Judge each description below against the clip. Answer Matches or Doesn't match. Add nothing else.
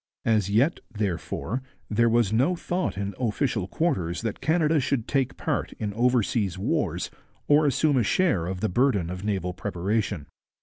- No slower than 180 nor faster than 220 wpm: Doesn't match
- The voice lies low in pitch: Matches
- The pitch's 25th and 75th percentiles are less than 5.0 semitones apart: Doesn't match